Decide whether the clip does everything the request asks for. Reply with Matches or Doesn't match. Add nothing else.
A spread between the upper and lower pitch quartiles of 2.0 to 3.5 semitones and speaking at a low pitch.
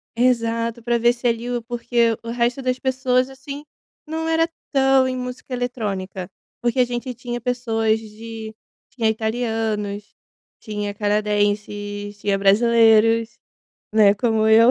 Doesn't match